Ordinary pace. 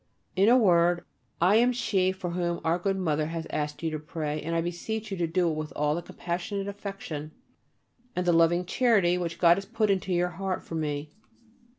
No: fast, 210 wpm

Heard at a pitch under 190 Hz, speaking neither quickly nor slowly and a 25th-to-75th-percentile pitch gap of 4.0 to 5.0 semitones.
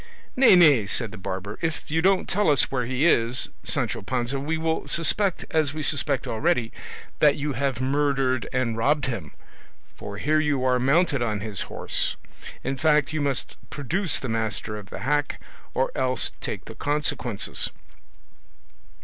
Yes: low, 135 Hz; average, 165 wpm; average, 4.7 semitones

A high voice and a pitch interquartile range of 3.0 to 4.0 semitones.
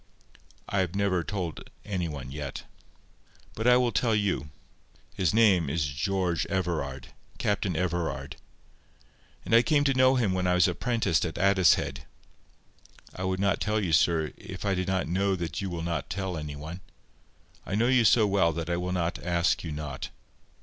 No: very low, 90 Hz; average, 3.4 semitones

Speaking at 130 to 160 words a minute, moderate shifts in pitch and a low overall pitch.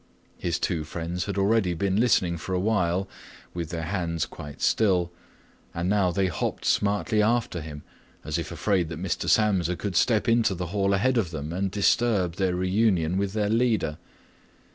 No: average, 175 wpm; average, 3.4 semitones; very low, 95 Hz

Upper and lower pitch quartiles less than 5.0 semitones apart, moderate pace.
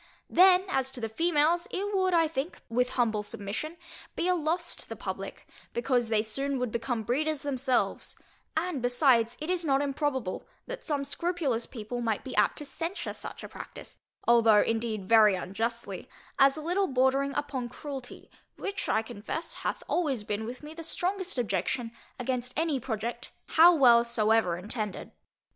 No: wide, 5.5 semitones; average, 165 wpm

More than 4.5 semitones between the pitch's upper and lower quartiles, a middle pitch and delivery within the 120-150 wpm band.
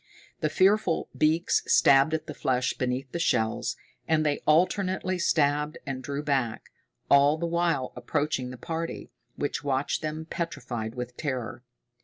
No: average, 3.9 semitones; medium, 145 Hz; average, 145 wpm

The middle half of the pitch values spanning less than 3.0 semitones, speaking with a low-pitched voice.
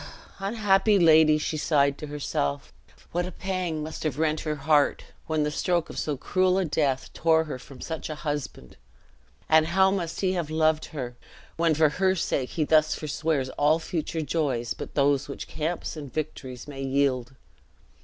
No: narrow, 2.6 semitones; medium, 155 Hz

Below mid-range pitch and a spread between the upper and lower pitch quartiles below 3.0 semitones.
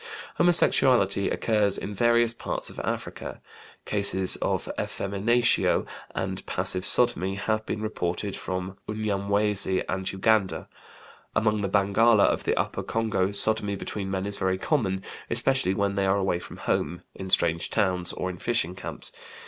Yes: low, 100 Hz; narrow, 2.4 semitones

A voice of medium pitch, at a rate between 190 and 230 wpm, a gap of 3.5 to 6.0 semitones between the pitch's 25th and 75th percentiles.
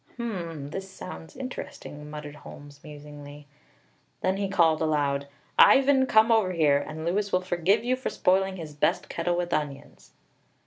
No: medium, 170 Hz; average, 150 wpm; average, 4.7 semitones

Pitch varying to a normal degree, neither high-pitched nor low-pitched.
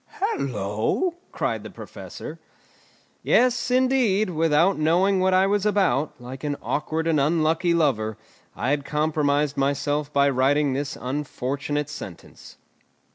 Yes: average, 4.8 semitones; medium, 150 Hz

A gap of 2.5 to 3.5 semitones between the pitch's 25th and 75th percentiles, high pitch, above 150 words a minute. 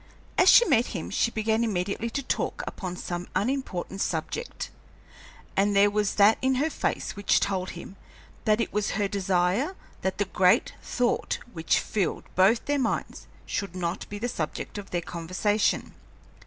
No: average, 3.9 semitones; high, 205 Hz; average, 165 wpm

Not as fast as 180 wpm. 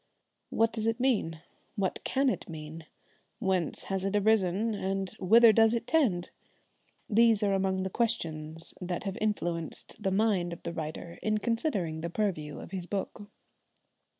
Yes: average, 155 wpm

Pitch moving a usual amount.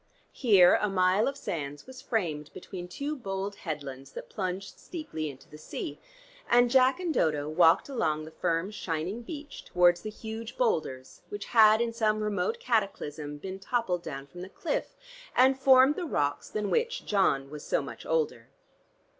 No: wide, 7.3 semitones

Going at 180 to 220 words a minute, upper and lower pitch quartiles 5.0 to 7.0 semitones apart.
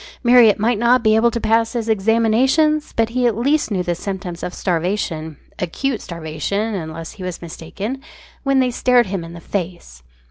Yes: average, 185 wpm; wide, 5.4 semitones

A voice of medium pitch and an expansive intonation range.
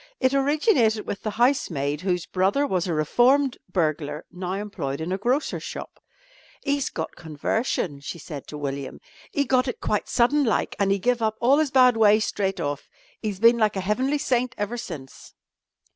No: high, 210 Hz; wide, 6.8 semitones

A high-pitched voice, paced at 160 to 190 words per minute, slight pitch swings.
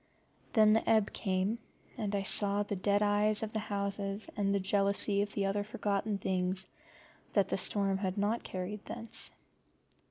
Yes: high, 200 Hz; average, 165 wpm; narrow, 1.2 semitones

